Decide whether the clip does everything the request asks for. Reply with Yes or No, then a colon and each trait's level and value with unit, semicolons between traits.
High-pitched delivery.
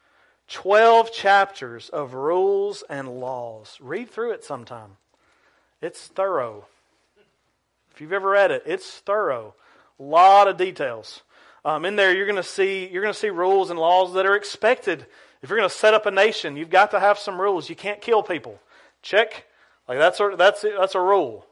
Yes: high, 200 Hz